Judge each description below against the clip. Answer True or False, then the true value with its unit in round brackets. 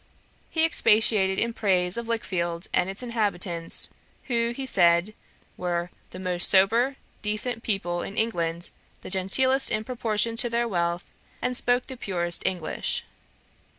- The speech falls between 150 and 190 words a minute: False (140 wpm)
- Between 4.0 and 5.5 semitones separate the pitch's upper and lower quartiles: True (4.8 semitones)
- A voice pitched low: False (205 Hz)